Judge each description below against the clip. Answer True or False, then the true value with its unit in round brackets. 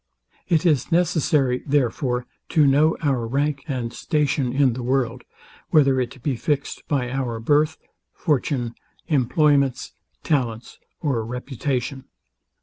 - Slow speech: True (120 wpm)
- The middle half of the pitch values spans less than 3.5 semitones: True (3.1 semitones)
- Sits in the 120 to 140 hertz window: True (135 Hz)